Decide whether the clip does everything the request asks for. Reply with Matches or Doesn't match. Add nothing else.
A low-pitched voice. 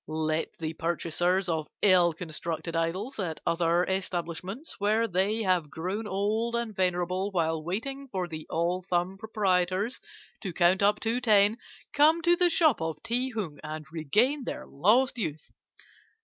Doesn't match